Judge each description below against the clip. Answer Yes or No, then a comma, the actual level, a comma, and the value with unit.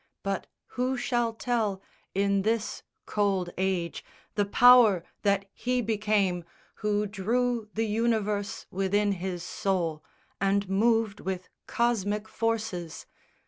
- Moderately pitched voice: No, high, 205 Hz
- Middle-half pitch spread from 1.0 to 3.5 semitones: Yes, average, 2.9 semitones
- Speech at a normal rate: No, slow, 110 wpm